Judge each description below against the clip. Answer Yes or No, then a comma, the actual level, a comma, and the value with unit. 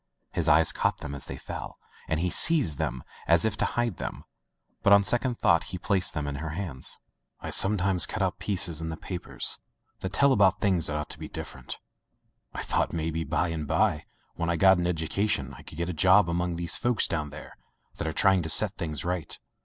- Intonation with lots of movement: No, average, 3.6 semitones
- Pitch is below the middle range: Yes, very low, 85 Hz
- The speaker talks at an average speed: No, fast, 220 wpm